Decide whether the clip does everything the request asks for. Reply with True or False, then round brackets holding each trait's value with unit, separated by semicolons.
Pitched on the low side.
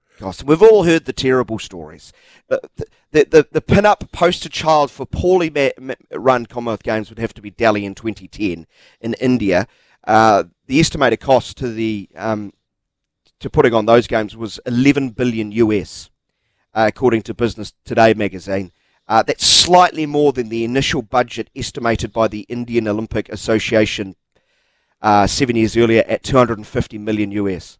True (115 Hz)